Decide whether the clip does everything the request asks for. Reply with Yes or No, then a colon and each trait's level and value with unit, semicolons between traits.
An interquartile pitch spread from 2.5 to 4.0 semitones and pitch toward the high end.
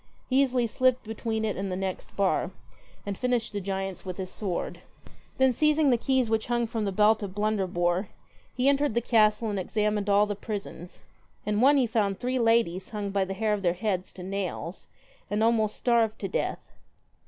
Yes: average, 3.3 semitones; high, 210 Hz